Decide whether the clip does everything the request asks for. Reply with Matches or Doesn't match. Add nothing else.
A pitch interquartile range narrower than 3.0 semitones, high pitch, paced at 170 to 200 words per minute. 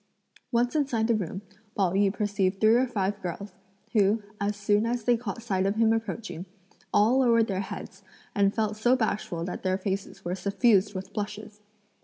Matches